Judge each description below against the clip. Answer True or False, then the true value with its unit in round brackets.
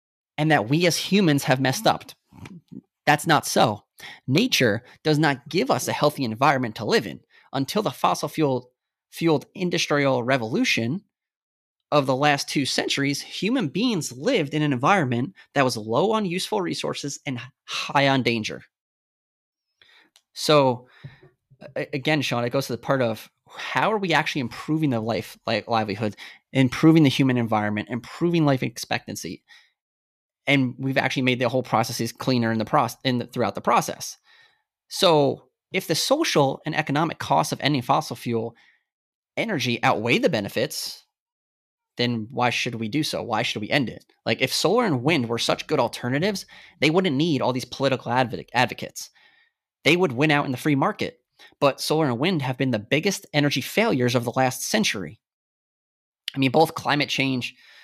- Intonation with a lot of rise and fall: False (3.9 semitones)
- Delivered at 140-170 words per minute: True (165 wpm)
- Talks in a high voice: False (140 Hz)